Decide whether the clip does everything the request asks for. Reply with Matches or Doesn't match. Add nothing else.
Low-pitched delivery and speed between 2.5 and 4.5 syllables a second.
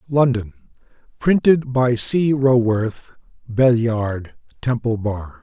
Matches